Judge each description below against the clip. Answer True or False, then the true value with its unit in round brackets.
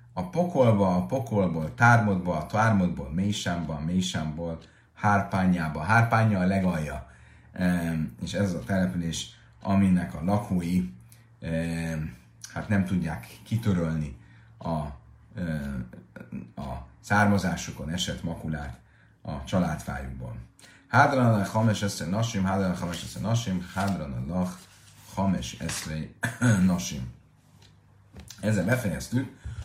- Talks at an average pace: False (100 wpm)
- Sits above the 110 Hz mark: False (90 Hz)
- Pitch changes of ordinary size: True (4.6 semitones)